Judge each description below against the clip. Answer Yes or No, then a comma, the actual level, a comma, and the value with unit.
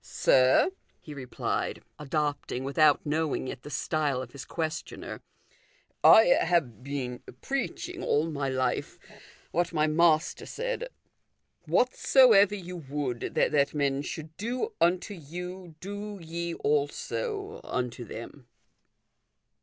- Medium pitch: Yes, medium, 155 Hz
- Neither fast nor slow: No, slow, 120 wpm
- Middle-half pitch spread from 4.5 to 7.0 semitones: Yes, average, 4.8 semitones